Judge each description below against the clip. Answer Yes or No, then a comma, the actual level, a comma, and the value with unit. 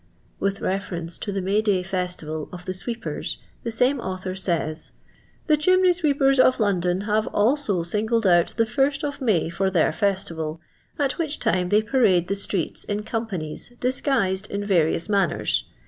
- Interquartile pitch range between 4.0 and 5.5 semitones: Yes, average, 5.1 semitones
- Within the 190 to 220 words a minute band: No, average, 170 wpm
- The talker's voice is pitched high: Yes, high, 200 Hz